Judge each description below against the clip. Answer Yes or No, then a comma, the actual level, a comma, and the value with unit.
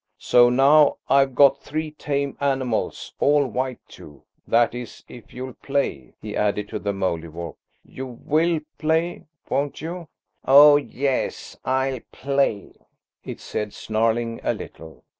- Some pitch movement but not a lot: Yes, average, 3.9 semitones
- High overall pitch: No, low, 130 Hz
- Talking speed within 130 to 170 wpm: Yes, slow, 135 wpm